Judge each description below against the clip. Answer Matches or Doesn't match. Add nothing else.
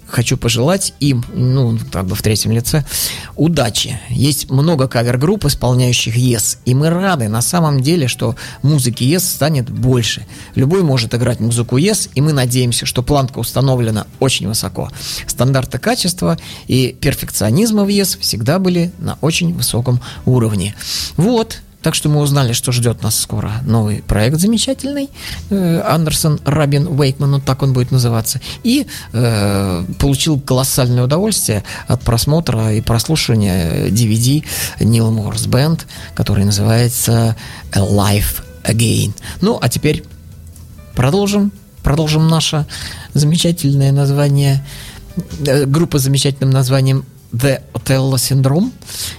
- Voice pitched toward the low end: Matches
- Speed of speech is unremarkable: Matches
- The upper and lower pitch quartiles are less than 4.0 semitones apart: Doesn't match